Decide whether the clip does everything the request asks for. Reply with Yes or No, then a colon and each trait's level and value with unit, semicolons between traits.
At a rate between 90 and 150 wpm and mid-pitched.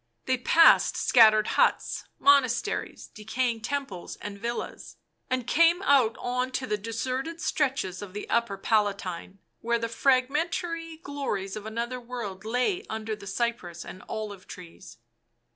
No: slow, 135 wpm; high, 235 Hz